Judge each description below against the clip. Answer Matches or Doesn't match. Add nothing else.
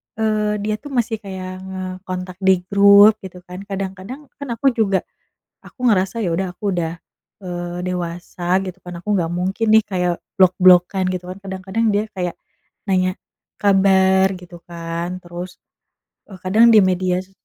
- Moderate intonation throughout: Doesn't match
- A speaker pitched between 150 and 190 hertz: Matches